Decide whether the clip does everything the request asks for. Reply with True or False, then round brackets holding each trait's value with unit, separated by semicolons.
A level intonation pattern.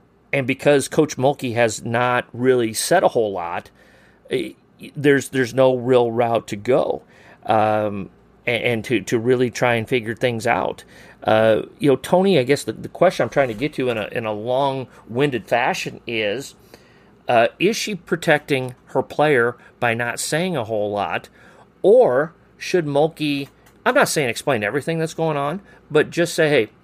False (4.2 semitones)